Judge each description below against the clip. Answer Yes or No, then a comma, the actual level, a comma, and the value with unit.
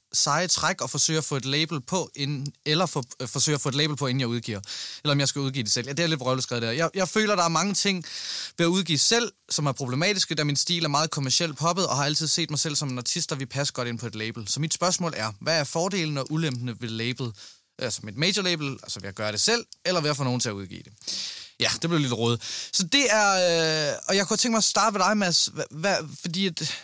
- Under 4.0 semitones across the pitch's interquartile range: No, average, 5.2 semitones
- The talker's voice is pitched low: No, medium, 150 Hz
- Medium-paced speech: No, fast, 285 wpm